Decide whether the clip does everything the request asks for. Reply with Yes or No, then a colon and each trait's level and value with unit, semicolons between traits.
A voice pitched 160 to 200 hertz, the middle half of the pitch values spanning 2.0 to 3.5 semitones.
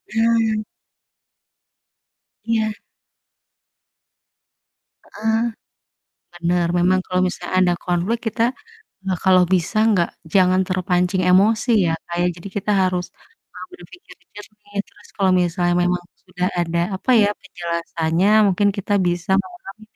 Yes: medium, 185 Hz; average, 3.0 semitones